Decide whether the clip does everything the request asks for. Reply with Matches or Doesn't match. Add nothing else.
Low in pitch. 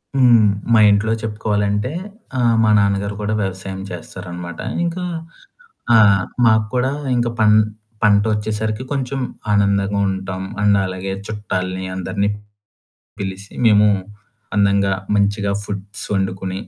Matches